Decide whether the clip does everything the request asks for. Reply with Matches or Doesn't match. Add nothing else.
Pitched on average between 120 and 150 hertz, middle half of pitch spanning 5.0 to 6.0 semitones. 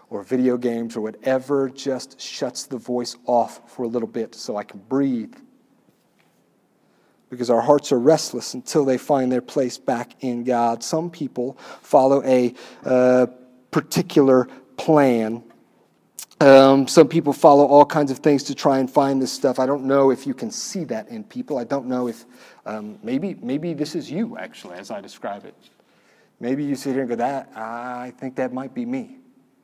Doesn't match